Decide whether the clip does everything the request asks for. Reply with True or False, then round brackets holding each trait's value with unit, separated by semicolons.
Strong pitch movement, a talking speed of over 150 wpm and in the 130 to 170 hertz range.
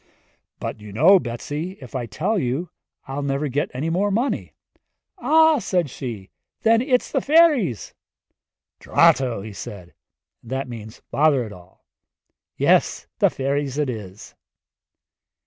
False (7.9 semitones; 135 wpm; 140 Hz)